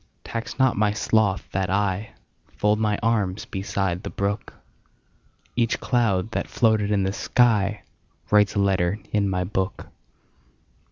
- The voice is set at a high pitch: No, low, 105 Hz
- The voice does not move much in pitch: Yes, narrow, 2.2 semitones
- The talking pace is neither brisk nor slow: No, slow, 120 wpm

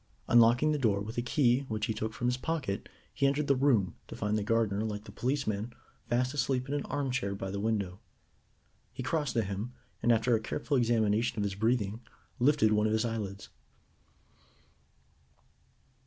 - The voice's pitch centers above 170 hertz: No, low, 115 Hz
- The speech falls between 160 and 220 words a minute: Yes, average, 180 wpm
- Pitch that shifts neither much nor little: Yes, average, 3.4 semitones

